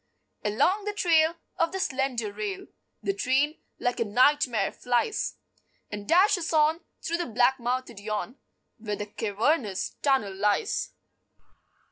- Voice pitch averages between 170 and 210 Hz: No, very high, 260 Hz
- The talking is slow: Yes, slow, 130 wpm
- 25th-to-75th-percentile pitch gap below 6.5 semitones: No, wide, 7.4 semitones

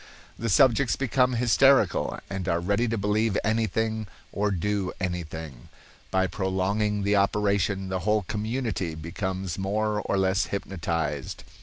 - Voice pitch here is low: Yes, low, 100 Hz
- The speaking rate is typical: No, slow, 130 wpm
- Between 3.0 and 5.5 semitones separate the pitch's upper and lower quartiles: No, narrow, 2.6 semitones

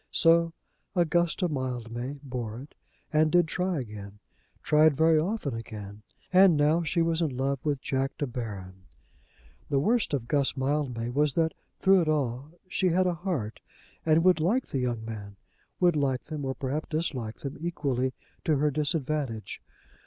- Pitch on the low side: No, medium, 145 Hz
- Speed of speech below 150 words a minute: No, average, 160 wpm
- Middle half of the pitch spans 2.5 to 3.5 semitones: No, average, 4.8 semitones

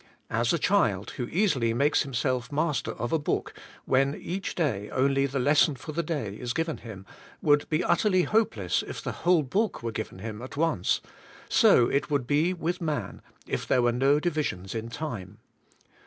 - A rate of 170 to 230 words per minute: Yes, average, 185 wpm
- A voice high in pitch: No, medium, 140 Hz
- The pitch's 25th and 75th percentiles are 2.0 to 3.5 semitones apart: No, average, 5.3 semitones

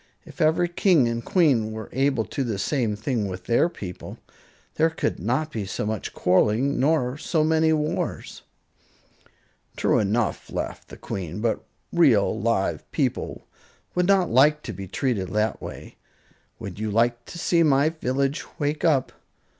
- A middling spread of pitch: No, wide, 6.3 semitones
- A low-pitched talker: Yes, low, 130 Hz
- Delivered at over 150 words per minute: Yes, average, 160 wpm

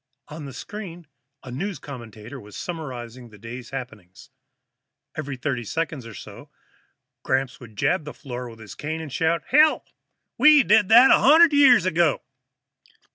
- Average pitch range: No, wide, 6.6 semitones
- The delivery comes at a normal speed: Yes, average, 160 wpm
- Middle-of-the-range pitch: Yes, medium, 145 Hz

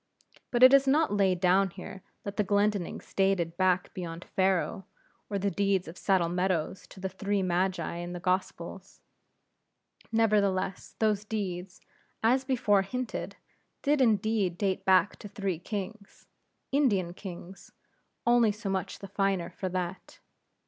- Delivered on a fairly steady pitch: Yes, narrow, 2.3 semitones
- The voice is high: Yes, high, 195 Hz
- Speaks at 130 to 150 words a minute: Yes, average, 140 wpm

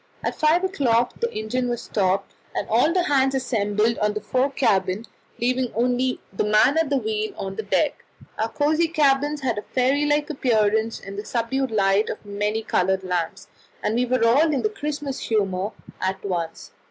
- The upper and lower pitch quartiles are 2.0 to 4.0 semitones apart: No, average, 5.3 semitones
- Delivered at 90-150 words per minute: No, average, 180 wpm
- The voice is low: No, high, 240 Hz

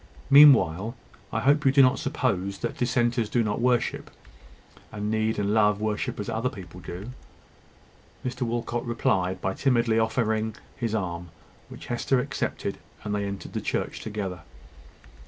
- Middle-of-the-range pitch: No, low, 110 Hz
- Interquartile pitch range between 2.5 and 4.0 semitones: Yes, average, 3.1 semitones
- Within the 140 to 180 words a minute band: Yes, average, 150 wpm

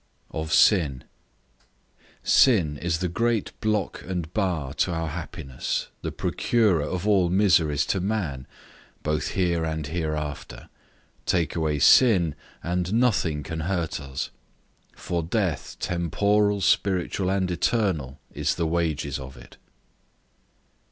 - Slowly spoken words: Yes, slow, 120 wpm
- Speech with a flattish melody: No, average, 4.0 semitones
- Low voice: Yes, very low, 85 Hz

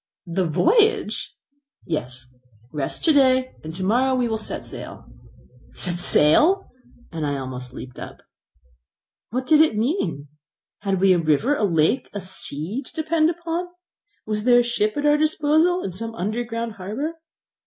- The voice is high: Yes, high, 225 Hz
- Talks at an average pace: Yes, average, 160 wpm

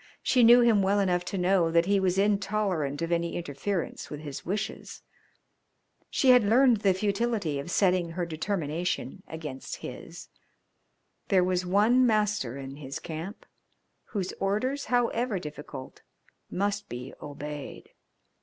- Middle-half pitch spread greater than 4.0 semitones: Yes, average, 4.6 semitones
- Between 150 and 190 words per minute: No, slow, 135 wpm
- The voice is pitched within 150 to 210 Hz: Yes, medium, 185 Hz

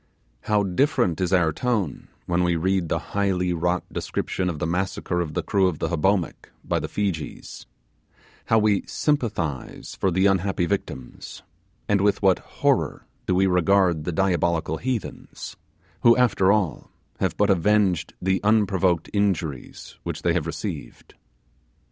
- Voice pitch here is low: Yes, very low, 95 Hz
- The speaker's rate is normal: Yes, average, 150 wpm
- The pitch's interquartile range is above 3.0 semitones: No, average, 2.7 semitones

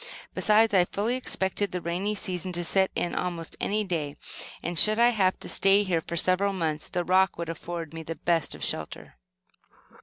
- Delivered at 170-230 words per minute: Yes, average, 190 wpm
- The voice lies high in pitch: No, medium, 180 Hz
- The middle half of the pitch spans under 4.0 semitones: Yes, average, 2.9 semitones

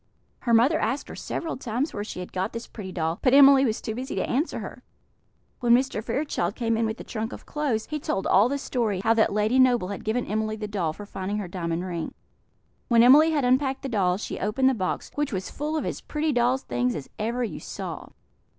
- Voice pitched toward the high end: Yes, high, 230 Hz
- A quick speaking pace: Yes, fast, 230 wpm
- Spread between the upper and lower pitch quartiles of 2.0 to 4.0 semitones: No, average, 4.6 semitones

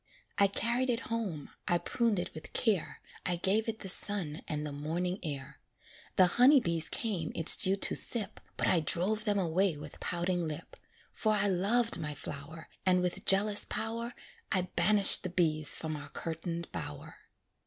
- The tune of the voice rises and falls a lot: No, average, 4.6 semitones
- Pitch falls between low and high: Yes, medium, 180 Hz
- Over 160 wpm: Yes, average, 175 wpm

